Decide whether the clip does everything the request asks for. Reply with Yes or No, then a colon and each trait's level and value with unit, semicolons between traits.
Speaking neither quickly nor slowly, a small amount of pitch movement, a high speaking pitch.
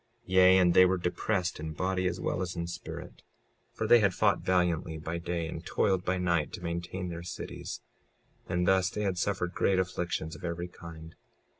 No: average, 195 wpm; narrow, 1.5 semitones; very low, 90 Hz